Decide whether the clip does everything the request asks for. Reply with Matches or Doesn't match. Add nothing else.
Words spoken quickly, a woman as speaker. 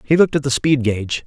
Doesn't match